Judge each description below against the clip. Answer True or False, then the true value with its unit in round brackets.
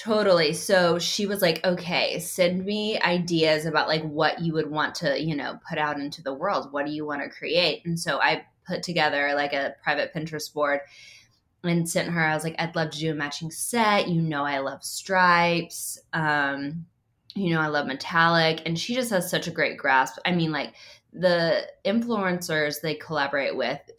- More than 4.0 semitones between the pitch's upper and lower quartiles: False (3.2 semitones)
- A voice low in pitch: False (160 Hz)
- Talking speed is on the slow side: False (200 wpm)